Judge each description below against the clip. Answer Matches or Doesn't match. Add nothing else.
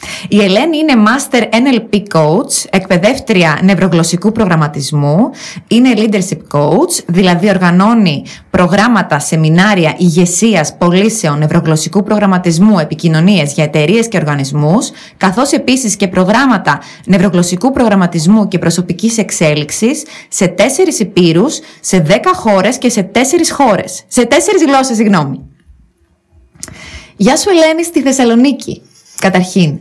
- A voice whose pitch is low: Doesn't match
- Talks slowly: Matches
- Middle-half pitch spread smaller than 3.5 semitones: Doesn't match